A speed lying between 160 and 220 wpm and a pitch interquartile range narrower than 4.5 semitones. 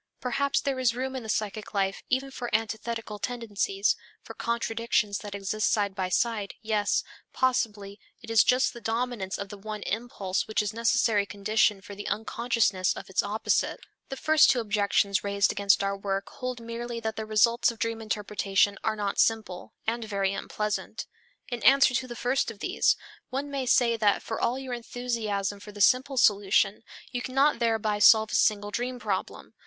Yes: average, 180 wpm; average, 2.9 semitones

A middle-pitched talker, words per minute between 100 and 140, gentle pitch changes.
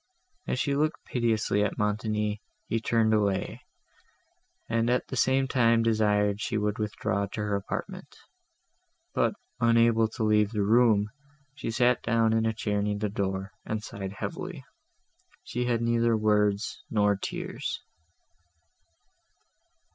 No: low, 110 Hz; slow, 135 wpm; narrow, 2.0 semitones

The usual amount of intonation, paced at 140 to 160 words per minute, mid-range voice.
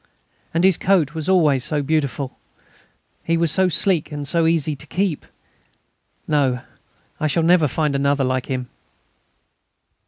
Yes: average, 3.0 semitones; average, 145 wpm; medium, 155 Hz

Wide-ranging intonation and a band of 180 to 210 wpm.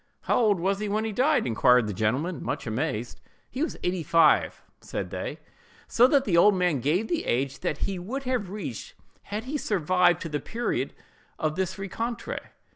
Yes: wide, 6.8 semitones; average, 190 wpm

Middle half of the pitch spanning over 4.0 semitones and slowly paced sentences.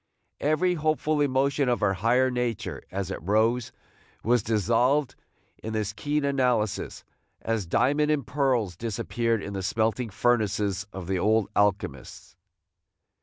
Yes: average, 4.7 semitones; slow, 130 wpm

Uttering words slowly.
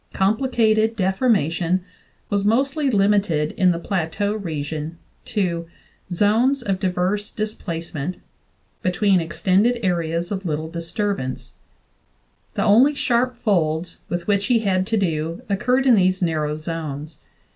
Yes: slow, 125 wpm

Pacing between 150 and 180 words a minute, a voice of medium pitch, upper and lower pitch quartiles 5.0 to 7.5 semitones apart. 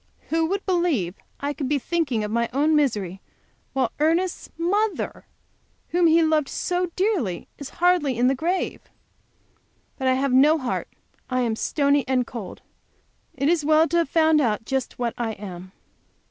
No: average, 165 wpm; very high, 285 Hz; average, 5.3 semitones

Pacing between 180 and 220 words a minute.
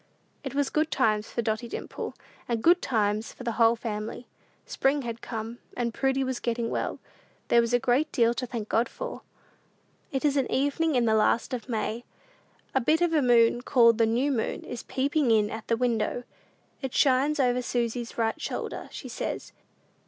Yes: average, 190 wpm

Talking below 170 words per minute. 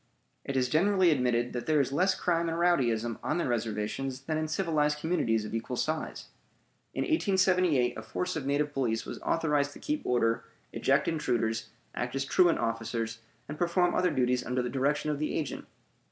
No: average, 180 wpm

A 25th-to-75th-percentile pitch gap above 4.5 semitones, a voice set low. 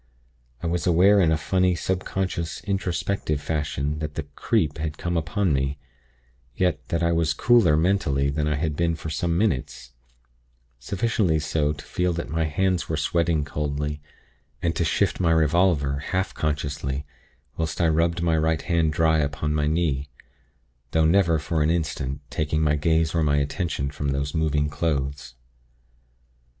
No: narrow, 2.5 semitones; very low, 80 Hz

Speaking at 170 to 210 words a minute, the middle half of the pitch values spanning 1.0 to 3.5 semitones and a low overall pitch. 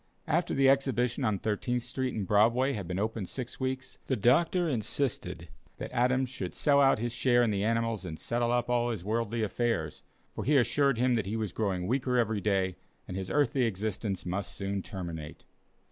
No: average, 190 wpm; average, 4.1 semitones; low, 115 Hz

